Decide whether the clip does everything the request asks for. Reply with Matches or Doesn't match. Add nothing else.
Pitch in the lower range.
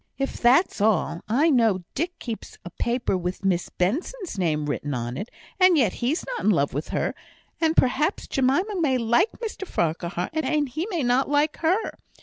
Doesn't match